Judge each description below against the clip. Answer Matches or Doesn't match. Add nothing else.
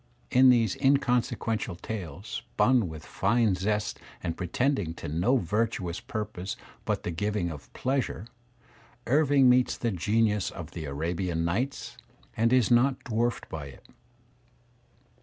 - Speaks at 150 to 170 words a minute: Doesn't match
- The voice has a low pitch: Matches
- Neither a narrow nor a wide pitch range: Doesn't match